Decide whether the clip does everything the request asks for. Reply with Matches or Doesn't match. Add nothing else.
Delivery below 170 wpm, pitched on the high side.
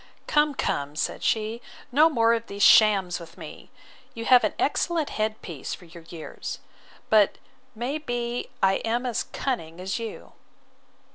Matches